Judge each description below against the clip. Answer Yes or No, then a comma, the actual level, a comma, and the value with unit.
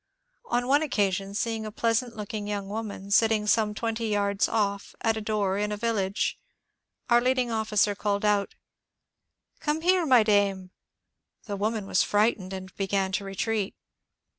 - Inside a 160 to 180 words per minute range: Yes, average, 165 wpm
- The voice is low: No, high, 210 Hz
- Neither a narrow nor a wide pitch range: No, narrow, 2.2 semitones